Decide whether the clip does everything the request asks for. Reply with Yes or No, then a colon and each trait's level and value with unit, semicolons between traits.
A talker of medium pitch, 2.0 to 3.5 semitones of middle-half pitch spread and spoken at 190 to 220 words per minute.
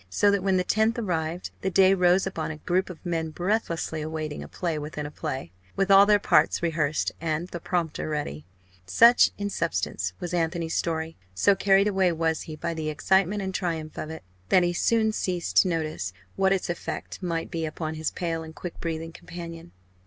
Yes: medium, 170 Hz; average, 3.1 semitones; average, 195 wpm